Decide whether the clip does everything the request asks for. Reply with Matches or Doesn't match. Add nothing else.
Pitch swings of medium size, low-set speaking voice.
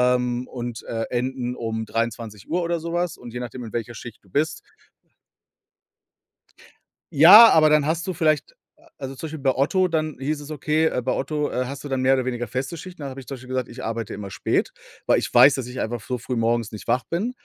Matches